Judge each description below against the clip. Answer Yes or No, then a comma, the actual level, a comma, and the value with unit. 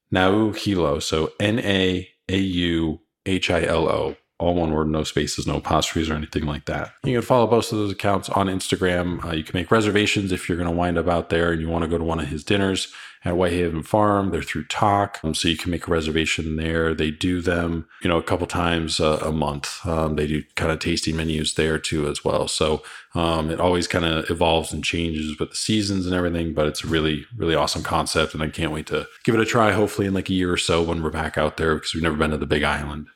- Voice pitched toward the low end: Yes, very low, 85 Hz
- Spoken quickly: Yes, fast, 250 wpm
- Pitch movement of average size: Yes, average, 3.0 semitones